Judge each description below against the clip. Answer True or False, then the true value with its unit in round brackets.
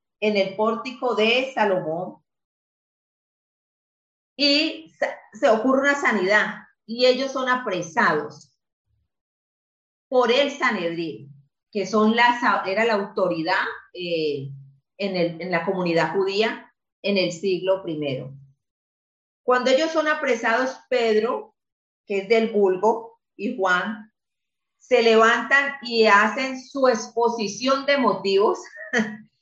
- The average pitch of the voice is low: False (220 Hz)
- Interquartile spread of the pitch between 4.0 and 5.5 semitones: True (5.2 semitones)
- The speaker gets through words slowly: True (110 wpm)